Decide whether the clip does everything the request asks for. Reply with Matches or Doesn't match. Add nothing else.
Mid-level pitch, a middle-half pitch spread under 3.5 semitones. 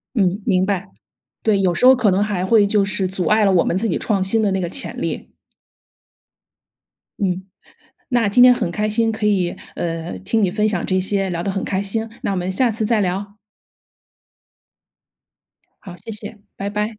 Doesn't match